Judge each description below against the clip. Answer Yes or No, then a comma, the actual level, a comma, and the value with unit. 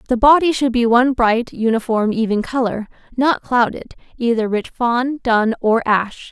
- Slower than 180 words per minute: Yes, average, 160 wpm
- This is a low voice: No, high, 240 Hz